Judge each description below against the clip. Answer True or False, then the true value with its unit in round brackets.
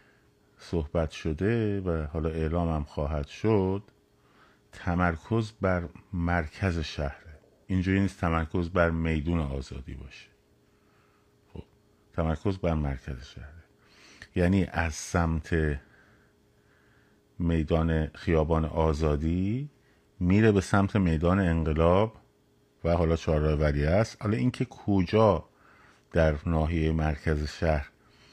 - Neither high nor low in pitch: False (85 Hz)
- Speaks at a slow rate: True (95 wpm)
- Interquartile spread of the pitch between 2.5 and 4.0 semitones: True (3.6 semitones)